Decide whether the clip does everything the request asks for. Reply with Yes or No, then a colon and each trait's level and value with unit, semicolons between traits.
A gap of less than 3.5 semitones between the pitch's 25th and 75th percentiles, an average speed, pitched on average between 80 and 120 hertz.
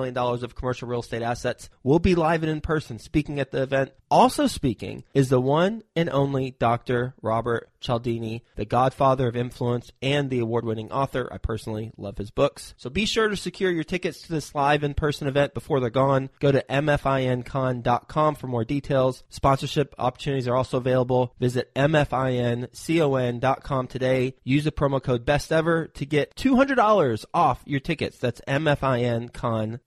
No: average, 3.1 semitones; average, 165 wpm; low, 130 Hz